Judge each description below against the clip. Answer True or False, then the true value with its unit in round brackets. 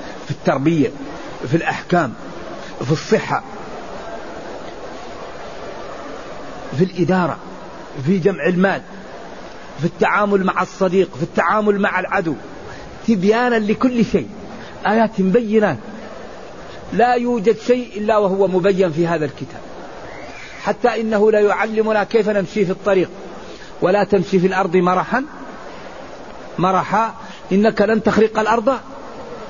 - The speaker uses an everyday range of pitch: True (3.1 semitones)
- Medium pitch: False (200 Hz)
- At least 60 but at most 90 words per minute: False (105 wpm)